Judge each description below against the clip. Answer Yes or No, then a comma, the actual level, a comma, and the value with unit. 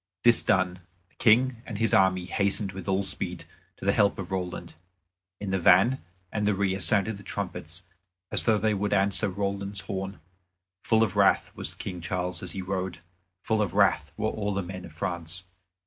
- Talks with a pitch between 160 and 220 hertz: No, very low, 95 Hz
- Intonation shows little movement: Yes, narrow, 2.0 semitones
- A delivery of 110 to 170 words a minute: No, average, 190 wpm